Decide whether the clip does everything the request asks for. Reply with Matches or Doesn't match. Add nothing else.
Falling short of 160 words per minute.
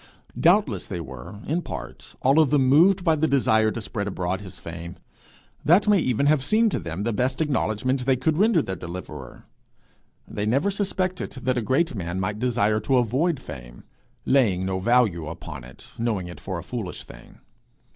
Doesn't match